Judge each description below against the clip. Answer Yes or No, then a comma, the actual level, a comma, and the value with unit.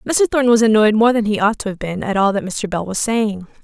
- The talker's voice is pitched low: No, high, 215 Hz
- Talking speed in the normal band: No, fast, 295 wpm